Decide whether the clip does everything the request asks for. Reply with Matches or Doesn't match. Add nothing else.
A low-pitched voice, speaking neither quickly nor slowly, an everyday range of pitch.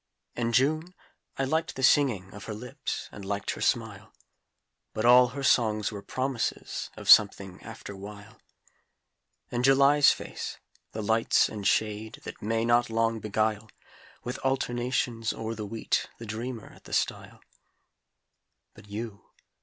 Matches